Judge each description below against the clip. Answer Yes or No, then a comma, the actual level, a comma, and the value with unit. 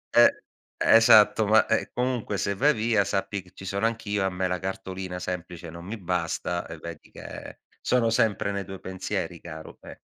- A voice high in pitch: No, very low, 95 Hz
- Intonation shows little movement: No, average, 3.1 semitones